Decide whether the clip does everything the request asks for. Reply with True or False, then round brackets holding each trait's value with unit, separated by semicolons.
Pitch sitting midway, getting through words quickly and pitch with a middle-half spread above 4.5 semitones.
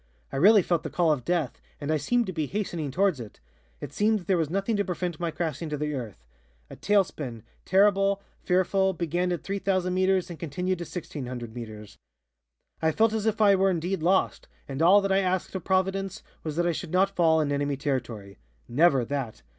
True (175 Hz; 210 wpm; 5.0 semitones)